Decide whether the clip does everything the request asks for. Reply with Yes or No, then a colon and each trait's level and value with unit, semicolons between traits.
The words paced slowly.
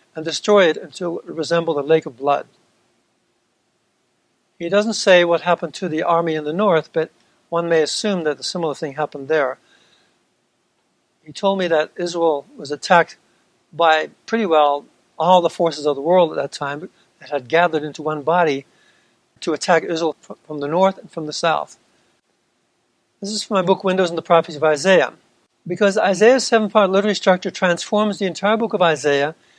No: average, 180 wpm